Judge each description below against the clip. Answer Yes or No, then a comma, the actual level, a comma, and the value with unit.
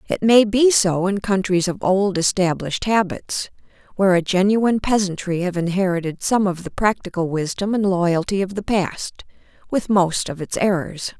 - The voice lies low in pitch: No, high, 190 Hz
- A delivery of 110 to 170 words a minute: Yes, average, 165 wpm